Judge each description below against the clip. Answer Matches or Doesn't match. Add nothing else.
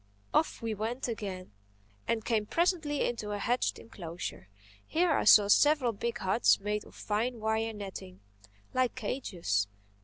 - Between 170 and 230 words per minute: Doesn't match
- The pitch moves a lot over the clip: Doesn't match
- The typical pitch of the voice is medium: Doesn't match